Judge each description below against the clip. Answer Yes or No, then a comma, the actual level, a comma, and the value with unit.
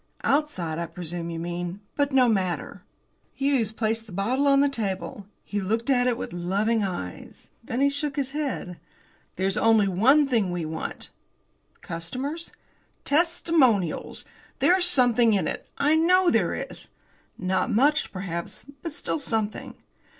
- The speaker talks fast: No, average, 145 wpm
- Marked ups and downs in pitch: Yes, wide, 7.2 semitones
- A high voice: Yes, high, 225 Hz